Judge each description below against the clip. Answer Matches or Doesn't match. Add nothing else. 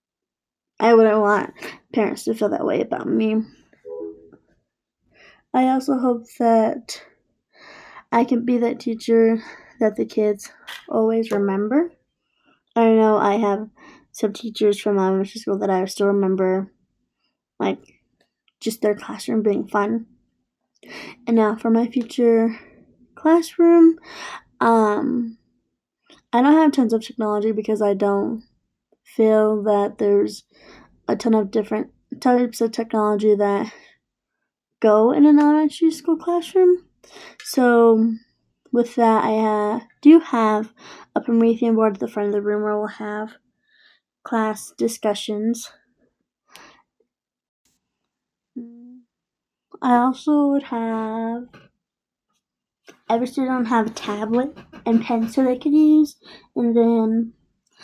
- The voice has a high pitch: Matches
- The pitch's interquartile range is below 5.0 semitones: Matches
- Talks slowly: Matches